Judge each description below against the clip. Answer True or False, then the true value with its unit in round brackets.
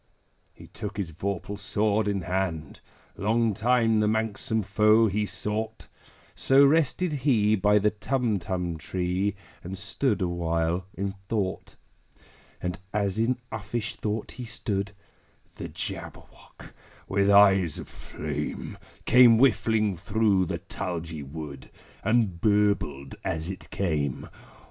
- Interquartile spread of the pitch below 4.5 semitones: True (3.5 semitones)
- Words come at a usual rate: False (120 wpm)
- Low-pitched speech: True (100 Hz)